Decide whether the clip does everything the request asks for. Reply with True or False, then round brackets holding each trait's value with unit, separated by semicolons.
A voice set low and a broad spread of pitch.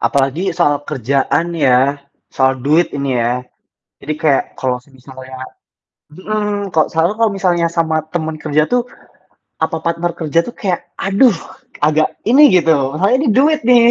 False (160 Hz; 5.7 semitones)